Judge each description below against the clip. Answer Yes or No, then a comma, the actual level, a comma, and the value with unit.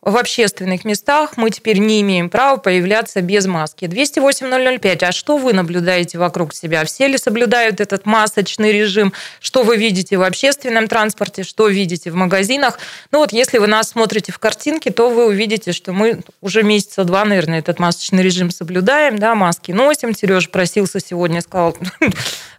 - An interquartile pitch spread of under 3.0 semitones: No, average, 4.1 semitones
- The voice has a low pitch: No, high, 205 Hz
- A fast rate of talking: Yes, fast, 165 wpm